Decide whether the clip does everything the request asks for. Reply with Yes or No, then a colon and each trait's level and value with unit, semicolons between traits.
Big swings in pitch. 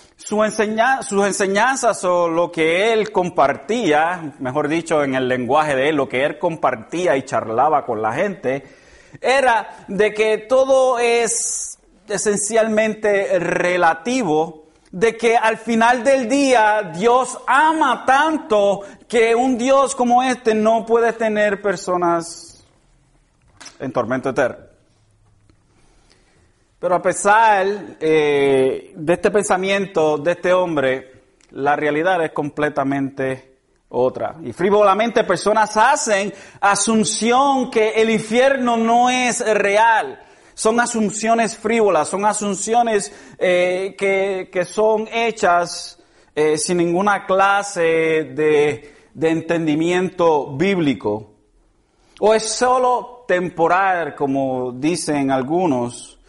Yes: wide, 6.2 semitones